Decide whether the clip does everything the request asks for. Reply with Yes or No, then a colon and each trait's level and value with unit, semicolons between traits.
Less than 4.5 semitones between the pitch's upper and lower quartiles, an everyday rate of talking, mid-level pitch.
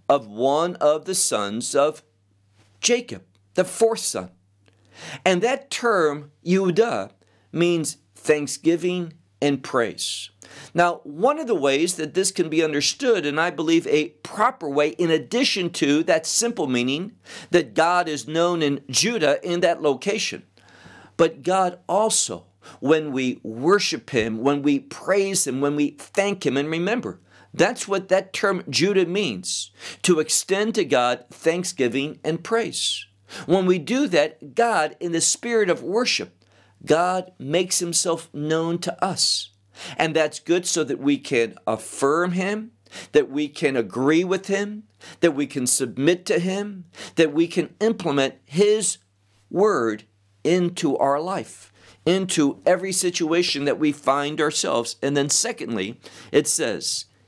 No: average, 5.3 semitones; average, 145 wpm; medium, 160 Hz